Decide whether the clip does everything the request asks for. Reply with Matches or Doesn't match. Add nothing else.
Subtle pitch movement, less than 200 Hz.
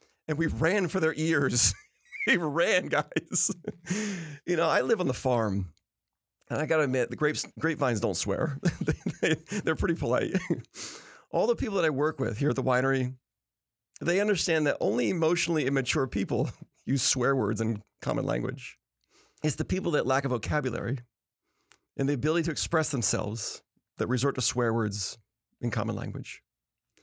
Doesn't match